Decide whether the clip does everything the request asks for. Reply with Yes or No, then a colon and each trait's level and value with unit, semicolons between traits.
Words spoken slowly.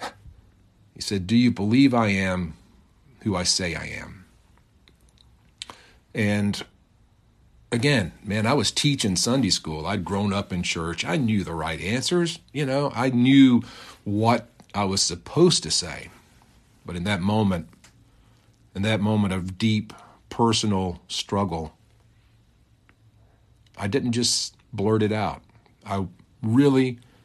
Yes: slow, 130 wpm